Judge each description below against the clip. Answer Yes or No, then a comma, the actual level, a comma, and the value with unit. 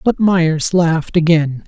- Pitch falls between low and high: Yes, medium, 165 Hz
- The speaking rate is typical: Yes, average, 145 wpm